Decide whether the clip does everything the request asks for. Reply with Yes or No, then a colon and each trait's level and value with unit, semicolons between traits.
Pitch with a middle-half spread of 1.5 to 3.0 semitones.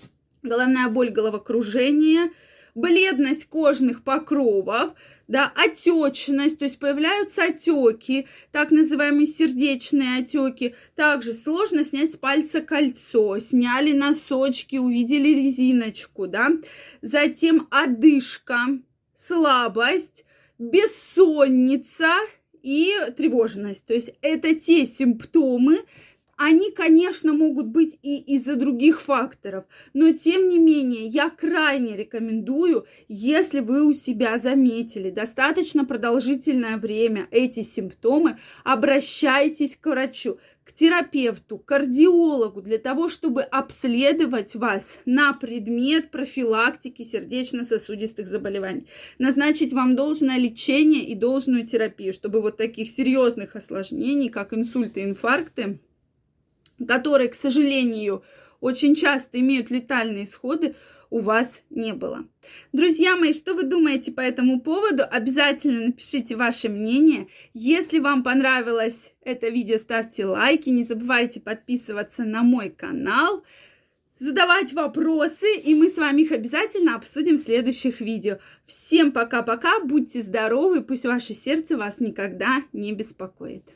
No: average, 4.4 semitones